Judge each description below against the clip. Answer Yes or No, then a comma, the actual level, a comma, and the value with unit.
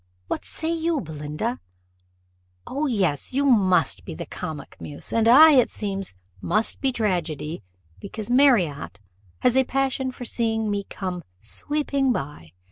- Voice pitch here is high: Yes, high, 220 Hz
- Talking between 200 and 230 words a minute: No, average, 140 wpm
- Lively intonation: Yes, wide, 7.7 semitones